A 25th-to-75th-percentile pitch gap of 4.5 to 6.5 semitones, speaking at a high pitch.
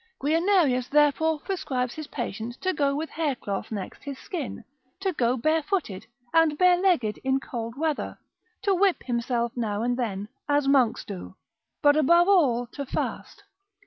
Yes: average, 5.1 semitones; very high, 280 Hz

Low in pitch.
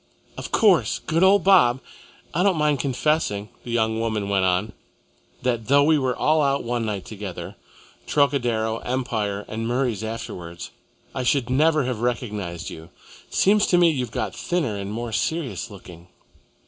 Yes: low, 120 Hz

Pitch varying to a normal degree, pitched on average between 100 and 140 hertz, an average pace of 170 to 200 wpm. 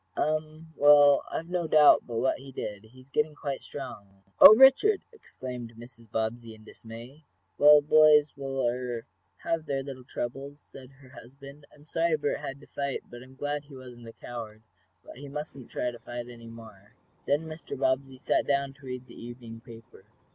Yes: average, 3.5 semitones; low, 135 Hz; average, 175 wpm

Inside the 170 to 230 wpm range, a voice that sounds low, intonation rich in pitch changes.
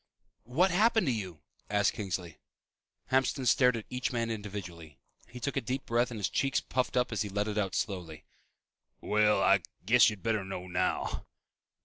No: average, 175 wpm; low, 110 Hz; average, 4.5 semitones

